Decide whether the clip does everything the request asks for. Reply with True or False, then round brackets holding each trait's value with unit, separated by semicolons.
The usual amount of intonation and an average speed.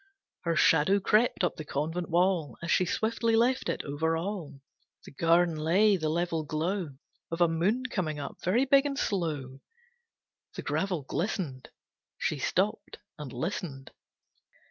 True (4.5 semitones; 145 wpm)